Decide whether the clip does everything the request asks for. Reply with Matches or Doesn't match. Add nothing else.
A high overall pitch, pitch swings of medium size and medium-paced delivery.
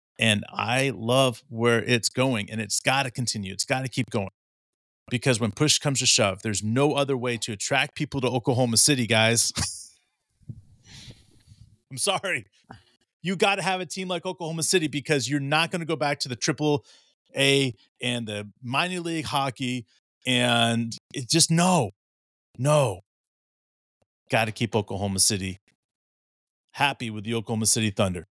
Doesn't match